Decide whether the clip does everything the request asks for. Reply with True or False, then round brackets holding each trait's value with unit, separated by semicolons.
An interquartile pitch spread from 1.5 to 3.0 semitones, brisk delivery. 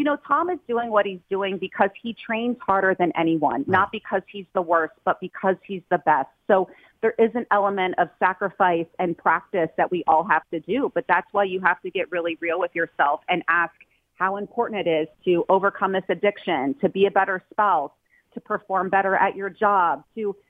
True (2.6 semitones; 210 wpm)